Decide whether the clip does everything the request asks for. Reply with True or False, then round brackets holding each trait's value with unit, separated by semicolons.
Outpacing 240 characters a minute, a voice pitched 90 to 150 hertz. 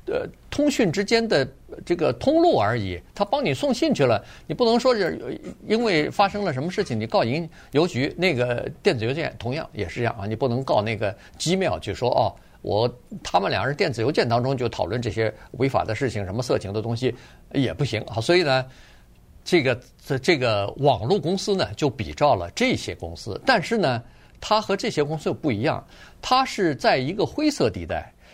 True (290 characters per minute; 135 Hz)